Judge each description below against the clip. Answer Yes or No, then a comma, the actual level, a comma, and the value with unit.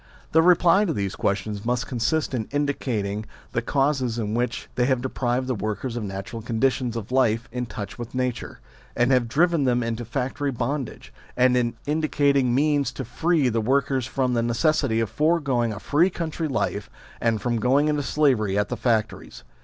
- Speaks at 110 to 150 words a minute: No, average, 175 wpm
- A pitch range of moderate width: Yes, average, 3.7 semitones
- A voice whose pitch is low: Yes, low, 125 Hz